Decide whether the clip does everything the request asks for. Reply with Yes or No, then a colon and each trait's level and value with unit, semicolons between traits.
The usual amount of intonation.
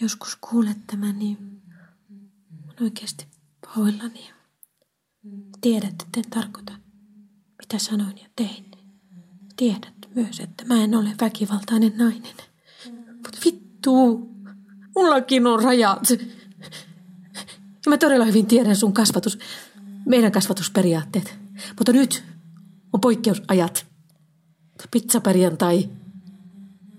Yes: average, 3.2 semitones